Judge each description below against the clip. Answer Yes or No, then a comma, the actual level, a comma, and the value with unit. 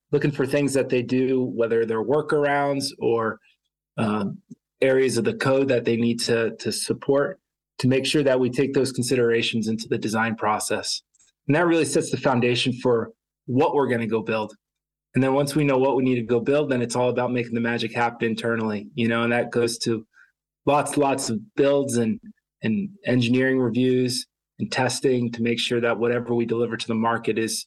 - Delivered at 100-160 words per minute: No, average, 200 wpm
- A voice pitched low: Yes, low, 125 Hz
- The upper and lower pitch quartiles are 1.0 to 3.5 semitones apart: Yes, average, 2.8 semitones